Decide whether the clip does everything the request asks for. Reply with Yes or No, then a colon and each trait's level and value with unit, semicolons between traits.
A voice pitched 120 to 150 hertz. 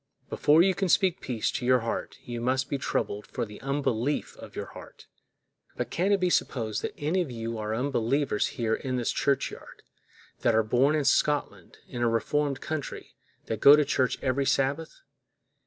Yes: low, 135 Hz